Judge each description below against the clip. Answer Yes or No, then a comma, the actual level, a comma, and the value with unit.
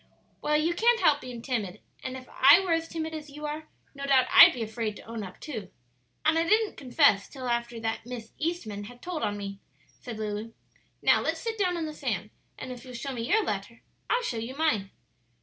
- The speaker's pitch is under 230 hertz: No, very high, 260 Hz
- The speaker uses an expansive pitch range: Yes, wide, 5.8 semitones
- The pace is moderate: No, fast, 220 wpm